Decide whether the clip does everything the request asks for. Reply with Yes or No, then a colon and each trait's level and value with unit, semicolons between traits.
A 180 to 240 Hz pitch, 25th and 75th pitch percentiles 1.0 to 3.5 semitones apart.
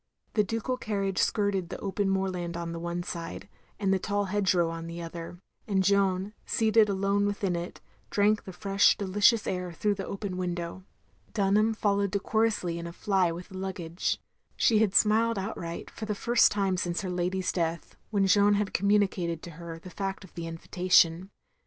Yes: high, 190 Hz; average, 2.8 semitones